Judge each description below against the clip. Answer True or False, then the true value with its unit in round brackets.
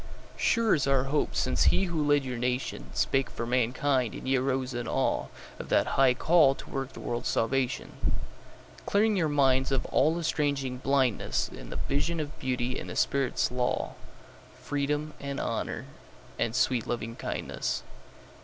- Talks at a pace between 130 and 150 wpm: True (145 wpm)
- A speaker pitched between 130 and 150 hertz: True (135 Hz)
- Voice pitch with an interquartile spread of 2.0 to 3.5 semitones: True (2.5 semitones)